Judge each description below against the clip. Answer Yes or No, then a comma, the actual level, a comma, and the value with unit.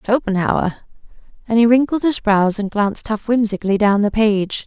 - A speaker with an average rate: Yes, average, 165 wpm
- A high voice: Yes, high, 215 Hz